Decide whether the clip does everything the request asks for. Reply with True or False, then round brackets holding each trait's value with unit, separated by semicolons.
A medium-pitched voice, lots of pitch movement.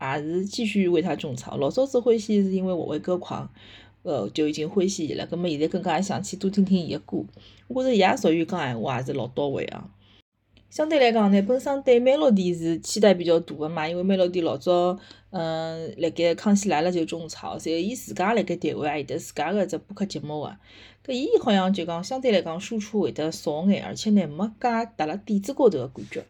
False (180 Hz; 4.4 semitones)